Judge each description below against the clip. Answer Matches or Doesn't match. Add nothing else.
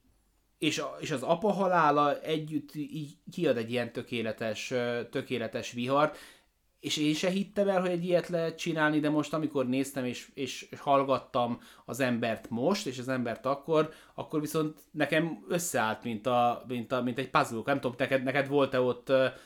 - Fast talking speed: Matches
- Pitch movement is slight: Doesn't match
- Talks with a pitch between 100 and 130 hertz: Doesn't match